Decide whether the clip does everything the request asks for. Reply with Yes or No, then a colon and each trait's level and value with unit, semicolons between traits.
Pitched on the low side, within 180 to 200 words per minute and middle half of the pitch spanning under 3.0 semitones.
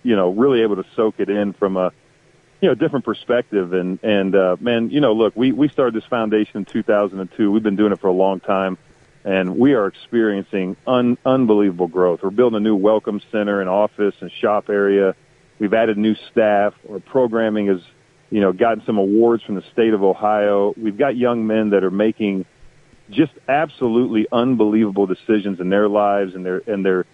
Yes: low, 105 Hz; average, 195 wpm; narrow, 2.5 semitones